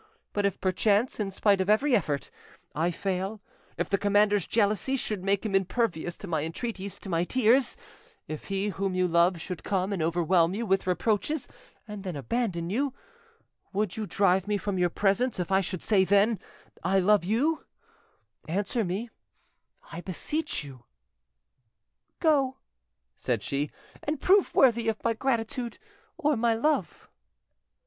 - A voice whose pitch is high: Yes, high, 200 Hz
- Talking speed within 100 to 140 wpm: No, average, 150 wpm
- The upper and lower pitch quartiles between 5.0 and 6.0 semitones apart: No, average, 4.1 semitones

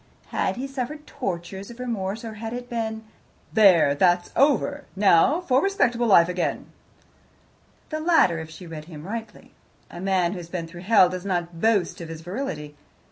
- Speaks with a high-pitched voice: Yes, high, 195 Hz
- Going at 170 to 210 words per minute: Yes, average, 175 wpm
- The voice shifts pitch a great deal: Yes, wide, 5.7 semitones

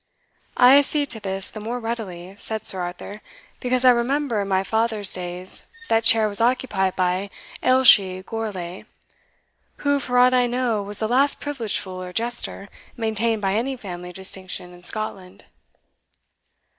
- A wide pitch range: No, average, 4.4 semitones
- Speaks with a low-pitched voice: No, high, 215 Hz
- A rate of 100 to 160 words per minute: Yes, average, 155 wpm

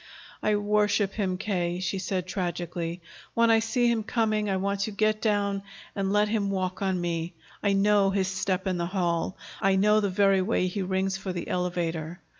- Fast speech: No, average, 195 wpm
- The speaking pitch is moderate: No, high, 195 Hz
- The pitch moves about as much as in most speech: No, narrow, 2.2 semitones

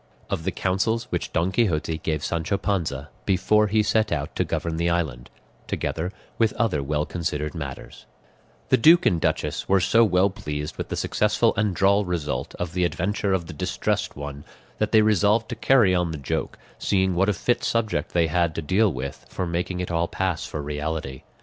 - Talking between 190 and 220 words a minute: Yes, average, 195 wpm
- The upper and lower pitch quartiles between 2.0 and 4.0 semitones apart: No, average, 4.6 semitones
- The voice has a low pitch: Yes, very low, 90 Hz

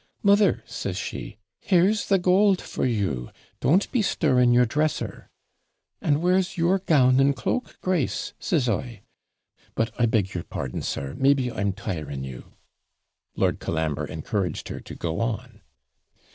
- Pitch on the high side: No, low, 125 Hz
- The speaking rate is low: No, average, 145 wpm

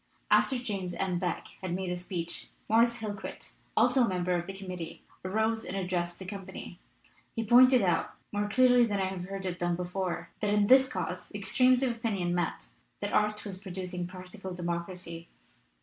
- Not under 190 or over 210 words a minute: No, average, 180 wpm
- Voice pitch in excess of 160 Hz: Yes, high, 190 Hz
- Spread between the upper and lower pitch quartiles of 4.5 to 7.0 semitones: No, average, 3.6 semitones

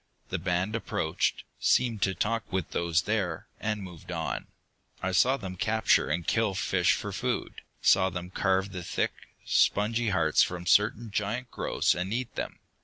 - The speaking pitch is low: Yes, very low, 95 Hz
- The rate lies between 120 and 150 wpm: No, average, 165 wpm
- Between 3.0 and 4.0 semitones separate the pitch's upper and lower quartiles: Yes, average, 3.7 semitones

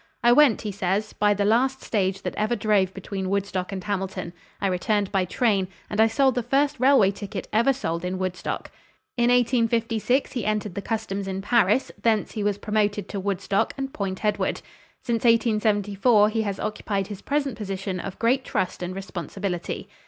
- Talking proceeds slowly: No, average, 180 wpm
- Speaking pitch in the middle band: No, high, 205 Hz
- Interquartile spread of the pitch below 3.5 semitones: Yes, average, 3.1 semitones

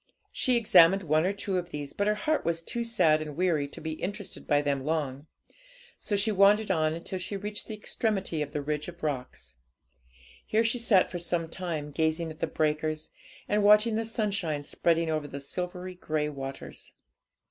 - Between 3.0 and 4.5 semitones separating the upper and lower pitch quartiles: No, average, 5.0 semitones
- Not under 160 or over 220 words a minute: Yes, average, 190 wpm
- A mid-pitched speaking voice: Yes, medium, 170 Hz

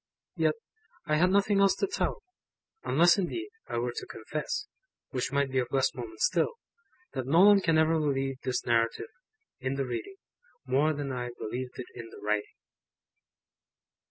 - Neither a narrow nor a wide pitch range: No, wide, 5.7 semitones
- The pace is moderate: Yes, average, 165 wpm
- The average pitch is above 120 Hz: Yes, medium, 140 Hz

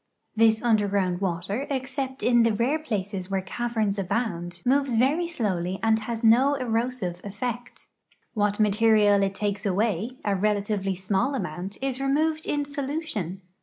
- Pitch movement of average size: Yes, average, 4.6 semitones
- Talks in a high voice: Yes, high, 220 Hz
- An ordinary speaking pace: Yes, average, 145 wpm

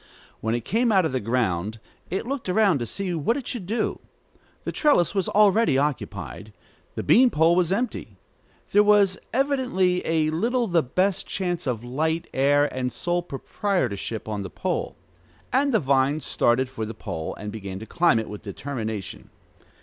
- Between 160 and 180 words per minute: Yes, average, 170 wpm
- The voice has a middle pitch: Yes, medium, 160 Hz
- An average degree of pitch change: No, wide, 8.8 semitones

